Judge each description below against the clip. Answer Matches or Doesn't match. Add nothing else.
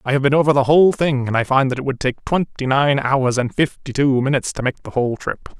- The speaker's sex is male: Matches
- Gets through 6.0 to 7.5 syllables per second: Matches